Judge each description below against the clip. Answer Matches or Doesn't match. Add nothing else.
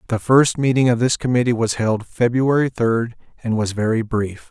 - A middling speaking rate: Matches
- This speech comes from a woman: Doesn't match